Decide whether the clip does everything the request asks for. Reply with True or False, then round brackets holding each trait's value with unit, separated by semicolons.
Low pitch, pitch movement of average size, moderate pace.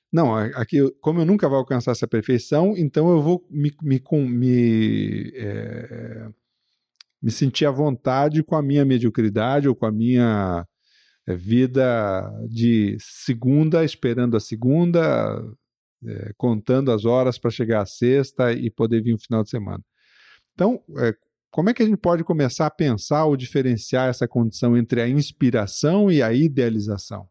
True (125 Hz; 4.4 semitones; 155 wpm)